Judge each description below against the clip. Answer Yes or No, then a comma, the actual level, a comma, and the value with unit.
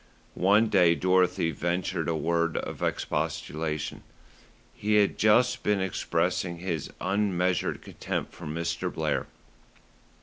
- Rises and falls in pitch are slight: No, average, 3.3 semitones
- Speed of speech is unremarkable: No, slow, 110 wpm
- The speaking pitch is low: Yes, very low, 90 Hz